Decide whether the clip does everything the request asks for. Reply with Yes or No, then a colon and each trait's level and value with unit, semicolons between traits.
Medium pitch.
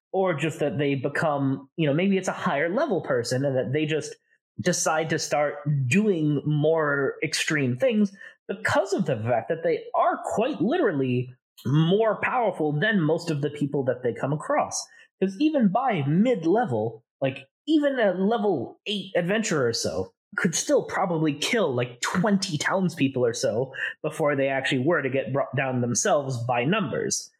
Yes: medium, 155 Hz